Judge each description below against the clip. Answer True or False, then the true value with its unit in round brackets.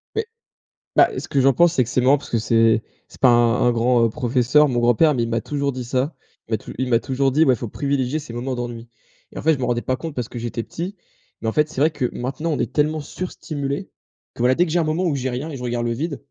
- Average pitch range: True (3.9 semitones)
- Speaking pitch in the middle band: False (130 Hz)